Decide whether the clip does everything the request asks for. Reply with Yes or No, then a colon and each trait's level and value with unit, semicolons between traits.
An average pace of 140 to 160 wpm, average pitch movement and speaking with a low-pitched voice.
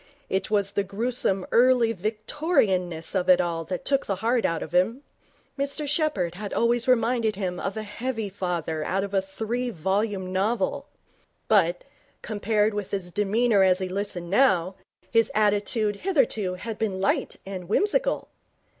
No: average, 155 wpm; average, 3.8 semitones; high, 205 Hz